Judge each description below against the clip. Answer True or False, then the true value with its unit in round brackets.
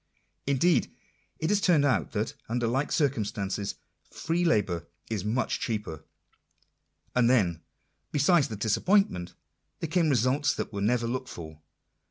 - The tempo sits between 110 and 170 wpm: True (140 wpm)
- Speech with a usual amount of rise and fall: False (6.5 semitones)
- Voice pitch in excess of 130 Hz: False (120 Hz)